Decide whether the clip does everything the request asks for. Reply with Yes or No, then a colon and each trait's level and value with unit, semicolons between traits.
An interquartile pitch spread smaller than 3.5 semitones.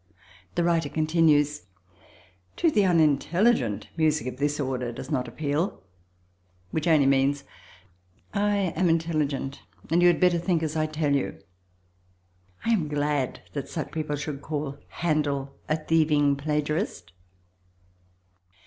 Yes: average, 2.7 semitones